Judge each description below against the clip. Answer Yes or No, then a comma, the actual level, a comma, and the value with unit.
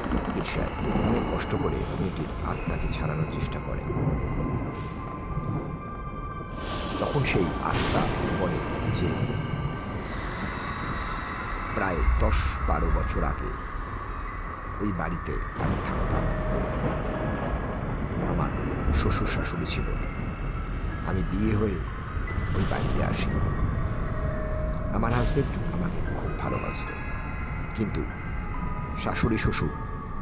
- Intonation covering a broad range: No, average, 4.5 semitones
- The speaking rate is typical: Yes, average, 80 wpm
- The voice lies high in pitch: No, very low, 90 Hz